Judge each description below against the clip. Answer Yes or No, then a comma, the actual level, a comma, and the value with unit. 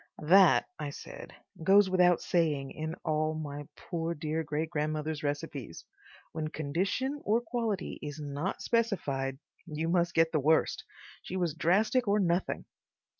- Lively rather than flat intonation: No, average, 3.9 semitones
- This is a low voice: No, medium, 160 Hz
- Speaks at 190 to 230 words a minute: No, average, 140 wpm